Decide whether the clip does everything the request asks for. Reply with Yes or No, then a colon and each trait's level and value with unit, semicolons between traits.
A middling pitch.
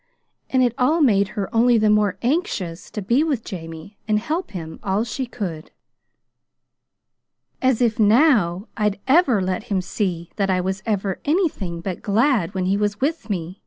No: high, 210 Hz